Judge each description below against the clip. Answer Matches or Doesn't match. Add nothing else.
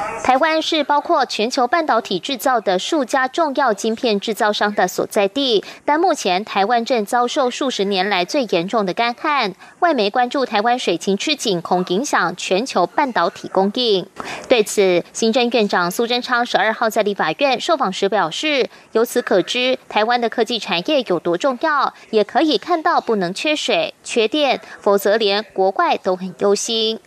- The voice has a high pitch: Matches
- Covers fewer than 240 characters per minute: Doesn't match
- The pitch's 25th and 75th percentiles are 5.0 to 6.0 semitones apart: Matches